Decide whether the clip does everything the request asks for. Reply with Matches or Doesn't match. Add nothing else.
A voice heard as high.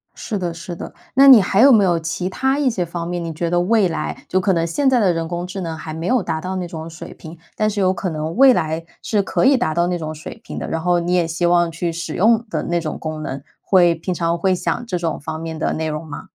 Doesn't match